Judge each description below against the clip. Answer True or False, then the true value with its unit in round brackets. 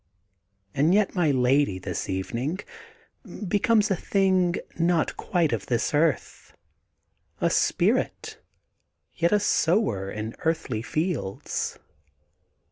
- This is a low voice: False (160 Hz)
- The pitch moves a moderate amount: False (7.4 semitones)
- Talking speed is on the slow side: True (105 wpm)